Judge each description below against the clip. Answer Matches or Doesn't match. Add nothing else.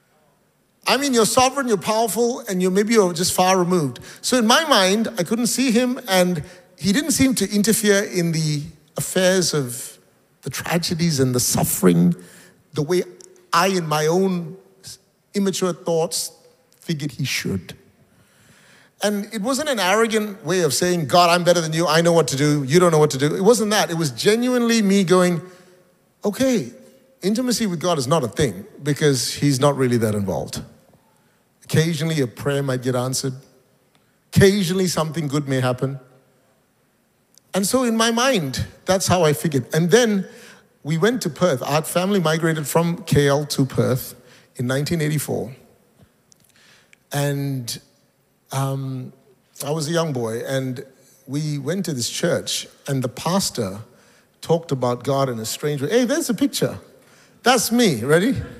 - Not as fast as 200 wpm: Matches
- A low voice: Doesn't match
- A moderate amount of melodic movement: Doesn't match